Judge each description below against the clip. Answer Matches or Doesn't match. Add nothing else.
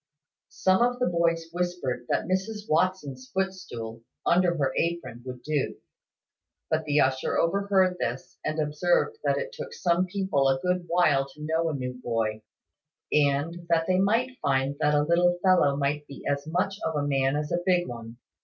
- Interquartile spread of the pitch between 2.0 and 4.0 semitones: Doesn't match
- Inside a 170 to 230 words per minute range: Matches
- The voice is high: Doesn't match